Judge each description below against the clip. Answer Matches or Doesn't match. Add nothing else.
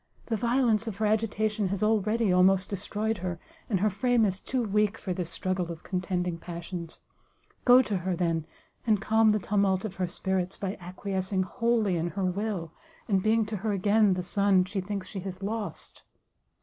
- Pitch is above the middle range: Matches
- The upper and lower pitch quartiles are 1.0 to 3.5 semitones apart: Matches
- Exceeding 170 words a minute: Matches